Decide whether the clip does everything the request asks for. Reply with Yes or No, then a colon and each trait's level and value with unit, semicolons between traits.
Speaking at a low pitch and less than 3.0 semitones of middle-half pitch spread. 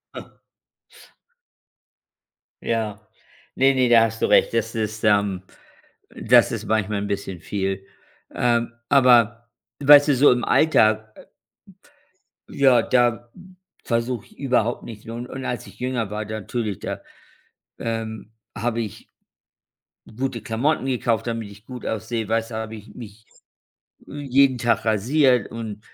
Yes: low, 115 Hz; narrow, 2.4 semitones